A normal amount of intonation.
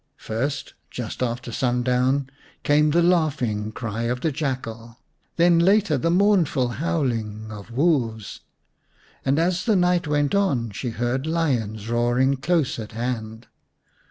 No: wide, 5.7 semitones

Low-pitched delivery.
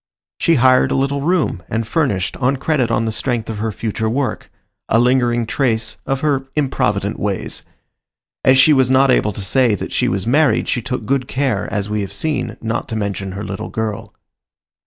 Yes: low, 120 Hz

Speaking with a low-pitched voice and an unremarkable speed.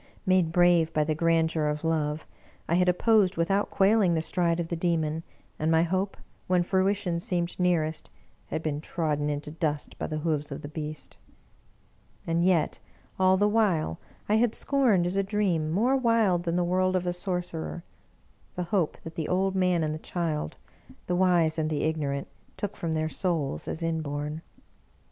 No: medium, 170 Hz; average, 175 wpm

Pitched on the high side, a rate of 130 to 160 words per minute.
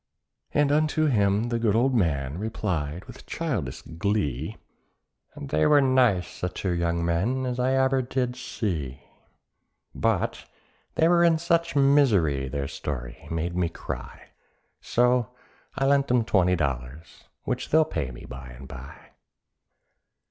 No: low, 100 Hz; average, 140 wpm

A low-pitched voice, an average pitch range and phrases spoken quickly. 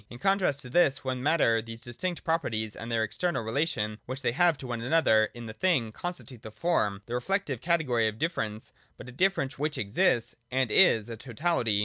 No: low, 125 Hz; wide, 6.6 semitones; fast, 210 wpm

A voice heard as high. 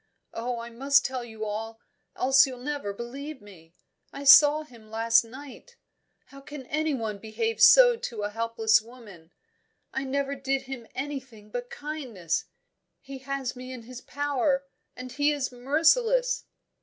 Yes: very high, 255 Hz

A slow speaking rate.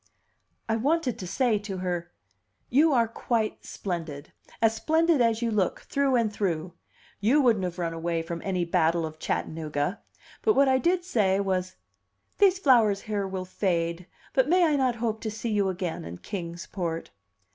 No: average, 175 wpm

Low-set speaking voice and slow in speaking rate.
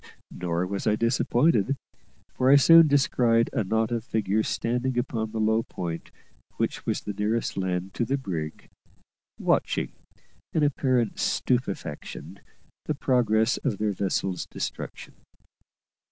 Yes: low, 110 Hz; slow, 130 wpm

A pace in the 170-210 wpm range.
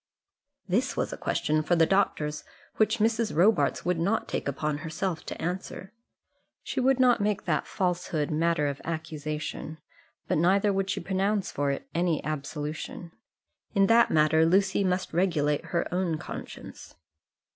No: average, 150 wpm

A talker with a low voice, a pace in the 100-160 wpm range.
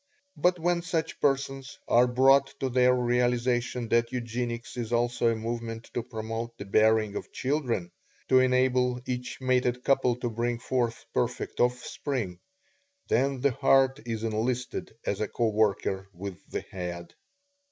Yes: low, 120 Hz; average, 145 wpm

